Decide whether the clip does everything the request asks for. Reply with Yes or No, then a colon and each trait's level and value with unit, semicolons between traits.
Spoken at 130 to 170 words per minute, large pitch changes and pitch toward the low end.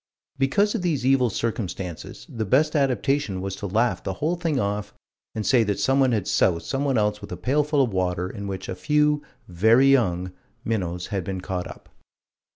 No: average, 185 wpm; wide, 6.4 semitones; low, 110 Hz